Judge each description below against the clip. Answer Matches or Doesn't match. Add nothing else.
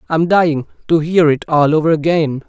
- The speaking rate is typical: Doesn't match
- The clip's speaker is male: Matches